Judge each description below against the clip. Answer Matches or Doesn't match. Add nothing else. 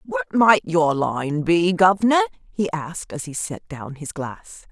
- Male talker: Doesn't match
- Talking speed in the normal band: Matches